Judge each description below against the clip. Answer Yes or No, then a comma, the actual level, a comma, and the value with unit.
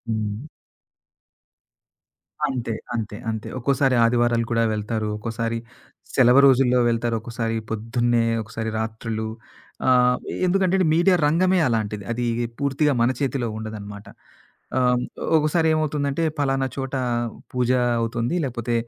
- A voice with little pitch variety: No, average, 3.2 semitones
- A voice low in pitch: Yes, low, 120 Hz